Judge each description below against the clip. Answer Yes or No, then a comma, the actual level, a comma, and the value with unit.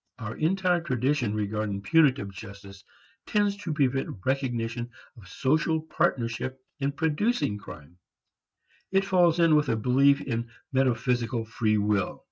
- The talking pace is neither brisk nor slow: No, slow, 125 wpm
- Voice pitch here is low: Yes, low, 130 Hz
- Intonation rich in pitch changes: Yes, wide, 6.1 semitones